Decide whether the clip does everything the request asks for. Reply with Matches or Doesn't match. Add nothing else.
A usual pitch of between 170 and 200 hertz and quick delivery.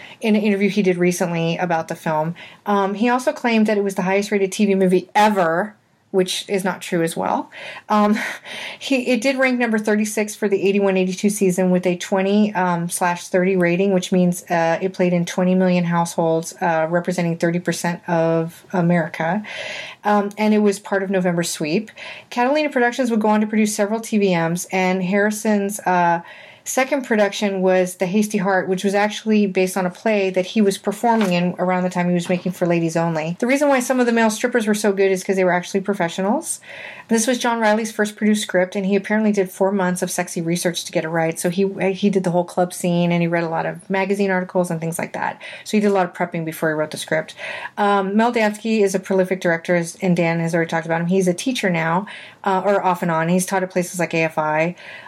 Matches